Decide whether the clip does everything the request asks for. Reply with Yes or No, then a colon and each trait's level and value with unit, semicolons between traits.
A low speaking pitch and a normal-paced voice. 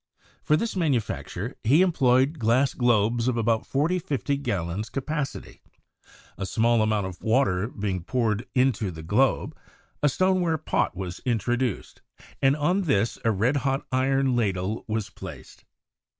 Yes: low, 120 Hz; average, 150 wpm